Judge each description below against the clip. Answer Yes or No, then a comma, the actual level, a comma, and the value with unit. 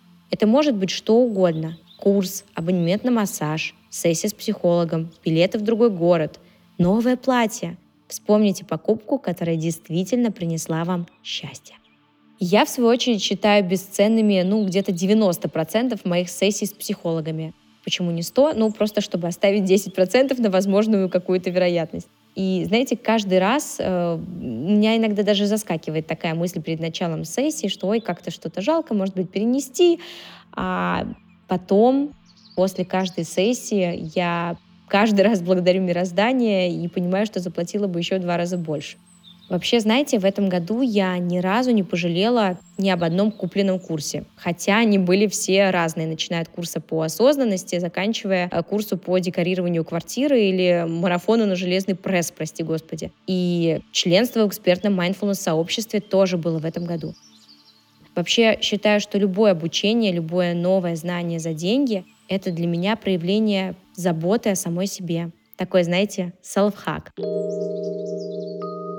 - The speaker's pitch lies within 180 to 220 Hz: Yes, high, 190 Hz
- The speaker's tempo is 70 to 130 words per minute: No, average, 140 wpm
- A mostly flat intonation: No, average, 3.2 semitones